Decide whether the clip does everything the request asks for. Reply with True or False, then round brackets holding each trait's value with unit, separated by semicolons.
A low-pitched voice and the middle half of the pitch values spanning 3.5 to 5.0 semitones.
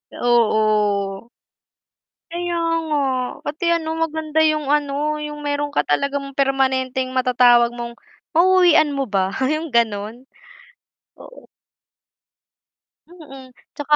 False (275 Hz; 4.2 semitones)